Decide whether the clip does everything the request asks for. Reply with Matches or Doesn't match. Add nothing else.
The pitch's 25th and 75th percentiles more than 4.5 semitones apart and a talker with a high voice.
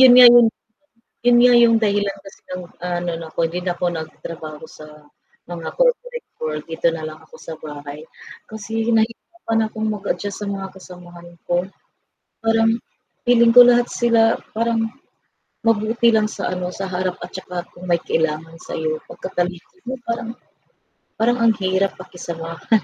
Matches